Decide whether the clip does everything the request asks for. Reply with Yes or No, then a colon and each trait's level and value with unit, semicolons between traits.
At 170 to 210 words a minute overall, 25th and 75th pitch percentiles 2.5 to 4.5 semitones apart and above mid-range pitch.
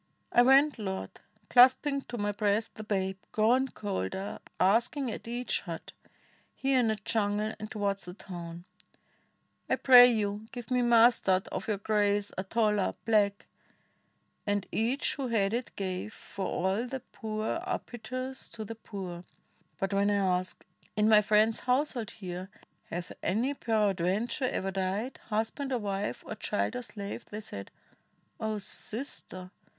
No: average, 160 wpm; average, 3.4 semitones; high, 215 Hz